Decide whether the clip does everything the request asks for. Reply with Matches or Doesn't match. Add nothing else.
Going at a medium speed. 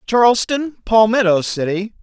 Doesn't match